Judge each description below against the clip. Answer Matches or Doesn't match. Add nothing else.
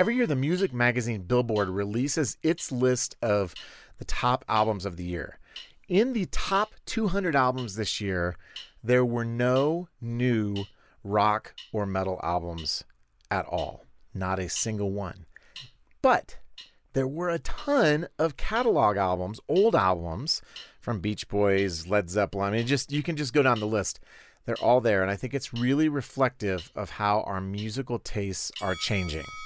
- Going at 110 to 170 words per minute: Matches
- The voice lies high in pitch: Doesn't match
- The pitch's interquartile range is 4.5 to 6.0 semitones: Matches